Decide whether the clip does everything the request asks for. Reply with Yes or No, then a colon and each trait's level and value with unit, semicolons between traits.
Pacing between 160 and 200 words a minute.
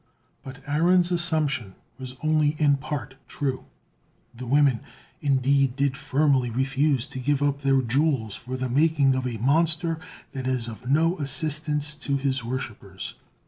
No: average, 145 wpm